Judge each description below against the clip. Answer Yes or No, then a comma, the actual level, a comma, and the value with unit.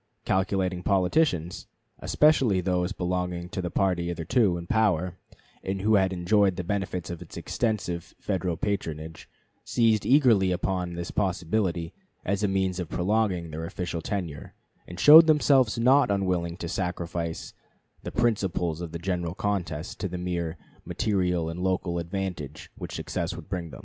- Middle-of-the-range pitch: No, very low, 90 Hz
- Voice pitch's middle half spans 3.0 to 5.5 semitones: No, narrow, 2.6 semitones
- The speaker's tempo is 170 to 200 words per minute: No, average, 150 wpm